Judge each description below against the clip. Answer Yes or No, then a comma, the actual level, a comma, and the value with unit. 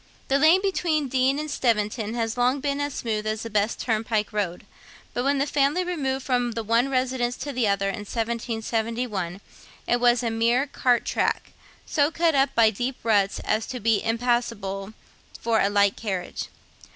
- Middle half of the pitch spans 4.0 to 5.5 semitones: No, average, 3.6 semitones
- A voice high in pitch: Yes, high, 235 Hz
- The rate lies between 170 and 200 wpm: Yes, average, 175 wpm